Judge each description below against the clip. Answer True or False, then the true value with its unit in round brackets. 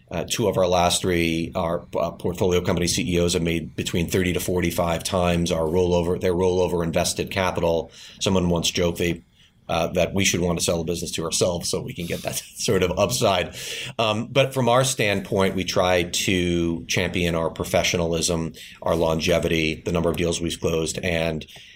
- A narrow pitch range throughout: True (1.7 semitones)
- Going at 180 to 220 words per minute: True (185 wpm)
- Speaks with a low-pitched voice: True (85 Hz)